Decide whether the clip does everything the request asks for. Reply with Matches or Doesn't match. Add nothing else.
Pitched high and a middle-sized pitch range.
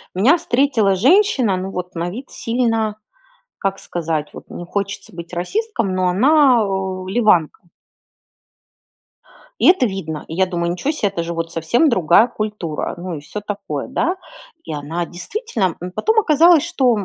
Doesn't match